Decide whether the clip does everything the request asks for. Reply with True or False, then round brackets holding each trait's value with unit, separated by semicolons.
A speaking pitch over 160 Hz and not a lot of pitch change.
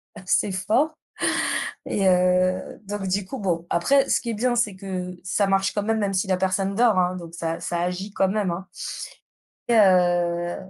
True (190 Hz; 2.2 semitones)